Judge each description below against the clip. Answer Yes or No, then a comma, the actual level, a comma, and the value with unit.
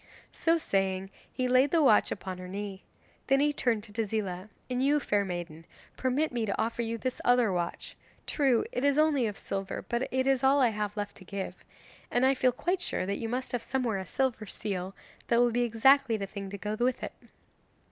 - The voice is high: Yes, high, 230 Hz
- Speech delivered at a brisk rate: Yes, fast, 215 wpm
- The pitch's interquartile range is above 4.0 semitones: Yes, average, 4.6 semitones